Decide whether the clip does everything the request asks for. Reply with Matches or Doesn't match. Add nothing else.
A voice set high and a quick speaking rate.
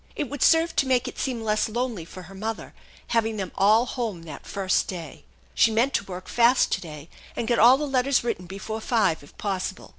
Matches